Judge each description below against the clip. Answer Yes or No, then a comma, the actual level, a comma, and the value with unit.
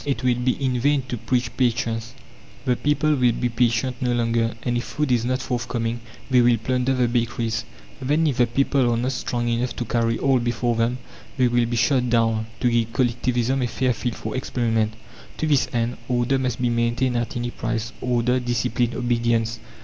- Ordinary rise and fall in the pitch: No, narrow, 1.5 semitones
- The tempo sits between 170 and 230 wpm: Yes, average, 195 wpm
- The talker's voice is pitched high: No, low, 120 Hz